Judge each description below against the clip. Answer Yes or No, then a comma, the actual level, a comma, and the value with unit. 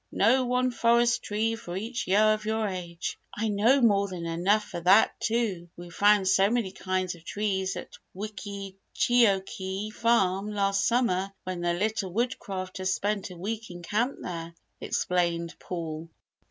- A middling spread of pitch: Yes, average, 3.2 semitones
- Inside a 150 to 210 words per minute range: Yes, average, 155 wpm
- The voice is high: Yes, high, 200 Hz